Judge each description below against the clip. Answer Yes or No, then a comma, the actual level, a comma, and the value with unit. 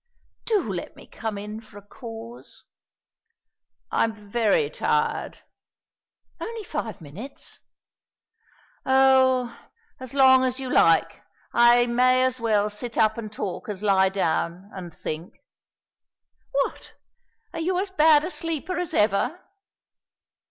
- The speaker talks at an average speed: No, slow, 125 wpm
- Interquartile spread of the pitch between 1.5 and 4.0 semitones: No, average, 4.6 semitones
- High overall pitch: Yes, high, 235 Hz